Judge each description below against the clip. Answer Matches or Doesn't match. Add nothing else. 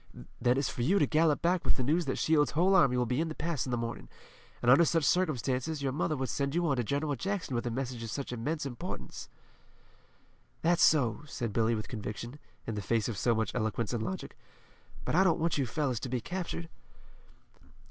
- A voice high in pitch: Doesn't match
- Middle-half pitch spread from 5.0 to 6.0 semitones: Matches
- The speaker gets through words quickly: Matches